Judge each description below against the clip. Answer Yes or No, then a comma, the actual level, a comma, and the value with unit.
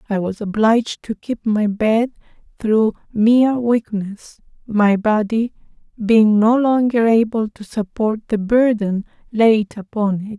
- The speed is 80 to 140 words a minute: Yes, slow, 135 wpm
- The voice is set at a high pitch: Yes, high, 220 Hz